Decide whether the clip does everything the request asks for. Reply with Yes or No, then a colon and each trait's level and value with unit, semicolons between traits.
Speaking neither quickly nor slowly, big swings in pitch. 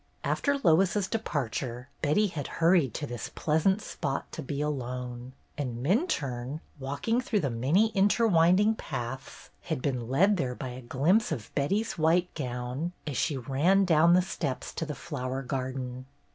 Yes: average, 155 wpm; wide, 6.1 semitones